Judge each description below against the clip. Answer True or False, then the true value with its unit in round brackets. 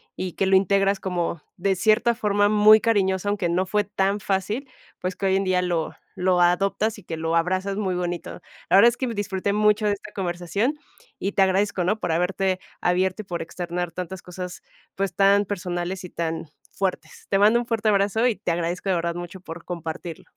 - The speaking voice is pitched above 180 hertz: True (190 Hz)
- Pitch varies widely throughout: False (2.5 semitones)